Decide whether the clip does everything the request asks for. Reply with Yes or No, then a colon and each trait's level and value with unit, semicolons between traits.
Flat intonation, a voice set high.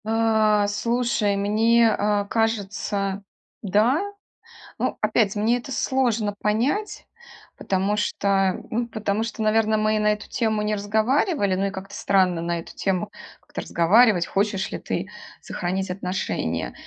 Yes: narrow, 2.3 semitones; high, 210 Hz